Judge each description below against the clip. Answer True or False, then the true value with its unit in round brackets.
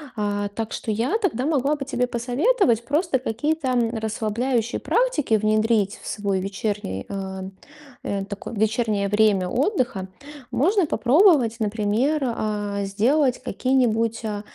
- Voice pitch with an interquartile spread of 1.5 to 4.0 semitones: False (4.4 semitones)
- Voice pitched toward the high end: True (225 Hz)